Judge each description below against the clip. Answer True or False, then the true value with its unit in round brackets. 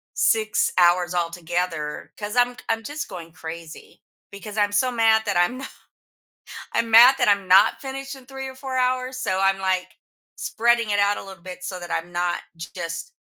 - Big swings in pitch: True (5.7 semitones)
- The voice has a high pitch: True (205 Hz)